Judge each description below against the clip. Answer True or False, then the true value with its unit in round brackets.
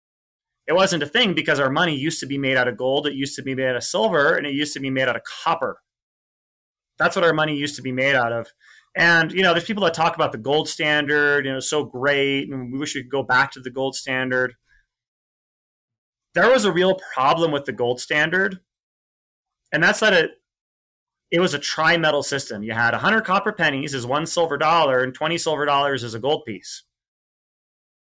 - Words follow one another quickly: True (220 wpm)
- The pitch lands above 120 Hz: True (140 Hz)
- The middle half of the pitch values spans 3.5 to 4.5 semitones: True (3.8 semitones)